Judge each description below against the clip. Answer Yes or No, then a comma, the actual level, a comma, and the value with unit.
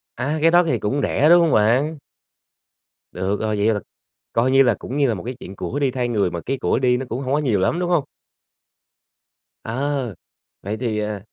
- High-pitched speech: No, low, 125 Hz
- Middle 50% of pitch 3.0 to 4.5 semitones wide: No, average, 5.0 semitones